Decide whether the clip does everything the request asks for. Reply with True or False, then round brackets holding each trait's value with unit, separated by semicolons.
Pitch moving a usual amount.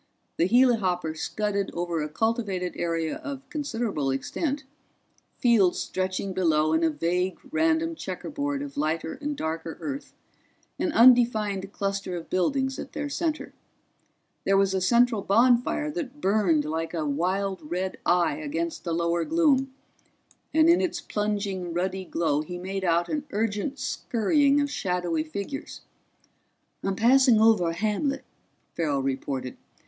False (7.3 semitones)